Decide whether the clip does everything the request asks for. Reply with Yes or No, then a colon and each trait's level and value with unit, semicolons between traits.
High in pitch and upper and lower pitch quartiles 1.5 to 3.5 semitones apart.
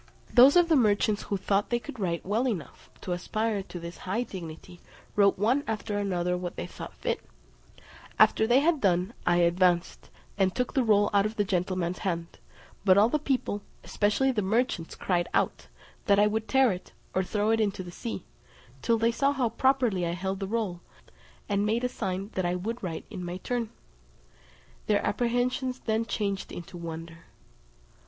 No: high, 205 Hz; average, 4.3 semitones